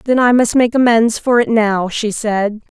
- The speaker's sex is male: No, female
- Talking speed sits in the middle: No, fast, 215 wpm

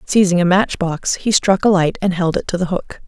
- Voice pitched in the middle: Yes, medium, 180 Hz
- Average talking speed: No, fast, 275 wpm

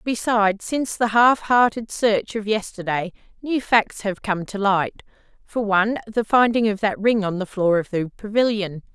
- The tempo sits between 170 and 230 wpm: Yes, average, 180 wpm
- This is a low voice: No, high, 210 Hz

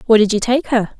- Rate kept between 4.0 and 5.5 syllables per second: No, 6.0 syllables/s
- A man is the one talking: No, female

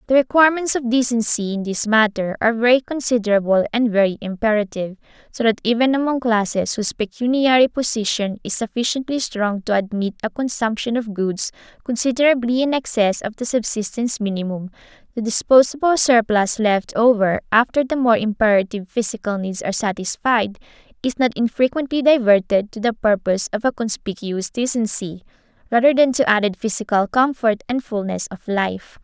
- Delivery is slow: No, average, 145 wpm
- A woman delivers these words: Yes, female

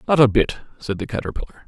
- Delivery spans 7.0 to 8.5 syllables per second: Yes, 7.6 syllables/s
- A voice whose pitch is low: Yes, low, 120 Hz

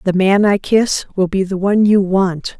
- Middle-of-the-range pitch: No, high, 195 Hz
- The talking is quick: Yes, fast, 230 wpm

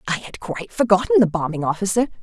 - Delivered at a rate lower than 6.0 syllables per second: No, 6.7 syllables/s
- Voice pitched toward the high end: Yes, high, 200 Hz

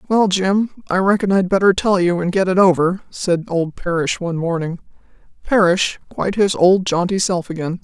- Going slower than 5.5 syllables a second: Yes, 5.2 syllables/s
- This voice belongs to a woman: Yes, female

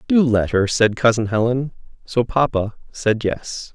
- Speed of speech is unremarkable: Yes, average, 160 wpm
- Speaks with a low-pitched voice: Yes, low, 120 Hz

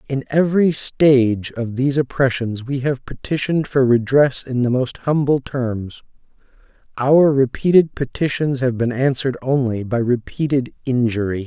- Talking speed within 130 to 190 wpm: Yes, slow, 135 wpm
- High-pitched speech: No, low, 130 Hz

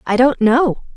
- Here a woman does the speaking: Yes, female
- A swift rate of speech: No, average, 190 wpm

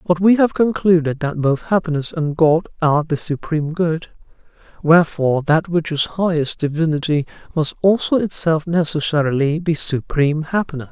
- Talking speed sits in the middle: Yes, average, 145 wpm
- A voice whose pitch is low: No, medium, 160 Hz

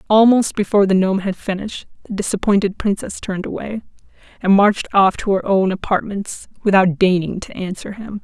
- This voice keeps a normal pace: Yes, average, 170 wpm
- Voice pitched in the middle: No, high, 200 Hz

